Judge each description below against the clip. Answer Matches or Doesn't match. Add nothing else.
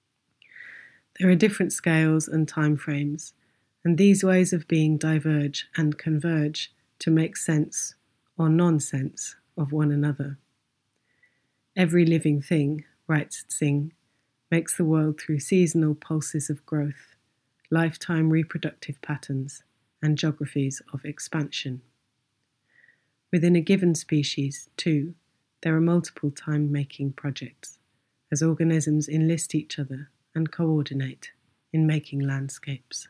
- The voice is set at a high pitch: Doesn't match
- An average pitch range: Doesn't match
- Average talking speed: Doesn't match